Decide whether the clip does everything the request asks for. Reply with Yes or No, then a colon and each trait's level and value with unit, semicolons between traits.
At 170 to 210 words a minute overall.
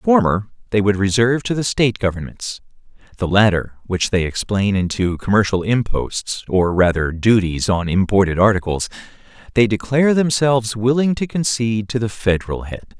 No: average, 150 wpm